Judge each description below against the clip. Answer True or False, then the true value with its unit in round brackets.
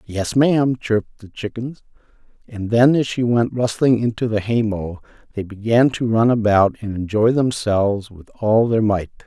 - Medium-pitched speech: False (110 Hz)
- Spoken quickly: False (175 wpm)